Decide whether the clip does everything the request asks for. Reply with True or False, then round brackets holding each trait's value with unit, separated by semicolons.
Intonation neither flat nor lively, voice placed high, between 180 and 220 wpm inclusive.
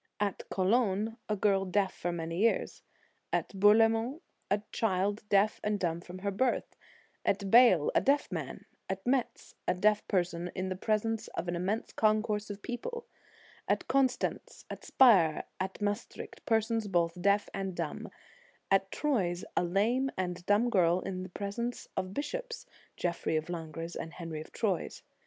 False (3.8 semitones; 200 Hz; 160 wpm)